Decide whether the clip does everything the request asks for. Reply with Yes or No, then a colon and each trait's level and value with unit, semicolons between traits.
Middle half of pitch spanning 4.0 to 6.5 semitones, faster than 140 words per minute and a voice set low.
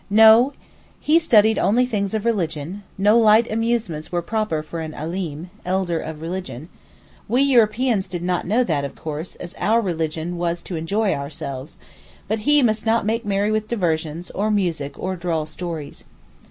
No: average, 5.2 semitones; average, 165 wpm; high, 190 Hz